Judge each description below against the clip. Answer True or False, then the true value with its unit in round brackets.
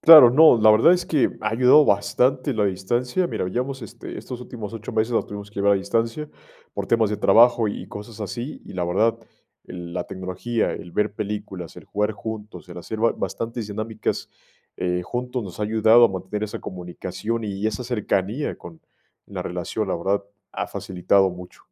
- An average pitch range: True (3.7 semitones)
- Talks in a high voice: False (110 Hz)